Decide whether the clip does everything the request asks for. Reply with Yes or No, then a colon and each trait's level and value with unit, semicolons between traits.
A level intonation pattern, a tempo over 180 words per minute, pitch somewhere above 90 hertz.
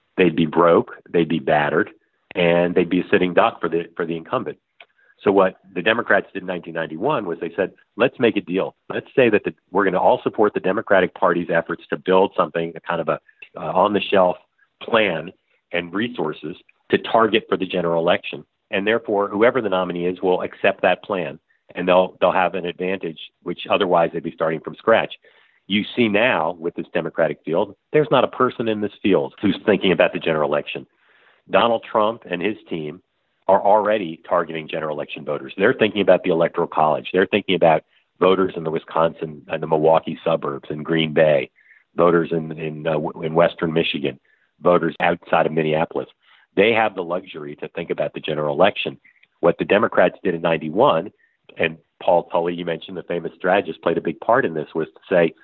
No: narrow, 2.3 semitones; average, 200 wpm; very low, 85 Hz